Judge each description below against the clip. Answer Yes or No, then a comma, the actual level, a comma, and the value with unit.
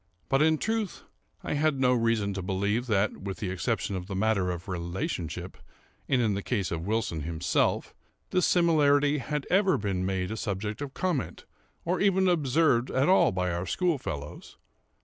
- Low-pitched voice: Yes, low, 110 Hz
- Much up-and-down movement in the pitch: Yes, wide, 8.0 semitones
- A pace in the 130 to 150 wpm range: No, average, 170 wpm